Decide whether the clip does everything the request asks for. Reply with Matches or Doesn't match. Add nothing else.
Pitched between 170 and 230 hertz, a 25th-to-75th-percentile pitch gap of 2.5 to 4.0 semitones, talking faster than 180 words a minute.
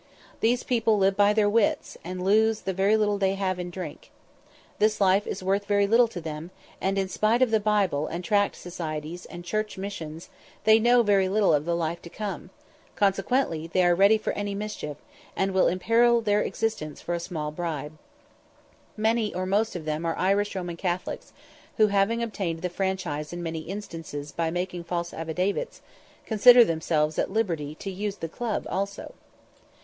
Doesn't match